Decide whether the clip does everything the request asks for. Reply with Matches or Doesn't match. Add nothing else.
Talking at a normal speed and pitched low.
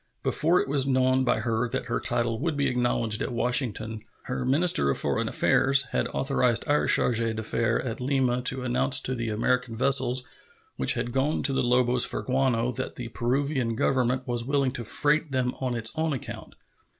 Matches